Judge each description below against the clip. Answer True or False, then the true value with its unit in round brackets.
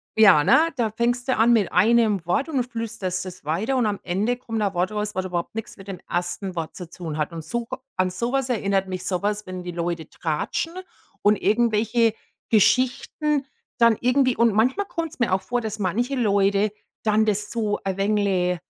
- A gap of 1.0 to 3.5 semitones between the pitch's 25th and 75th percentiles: False (4.2 semitones)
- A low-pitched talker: False (210 Hz)